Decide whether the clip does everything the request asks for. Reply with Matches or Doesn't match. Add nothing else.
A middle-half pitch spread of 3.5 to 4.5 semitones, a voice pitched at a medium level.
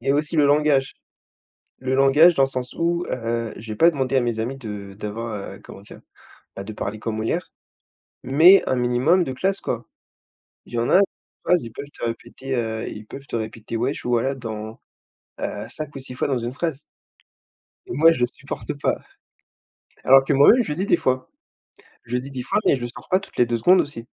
Doesn't match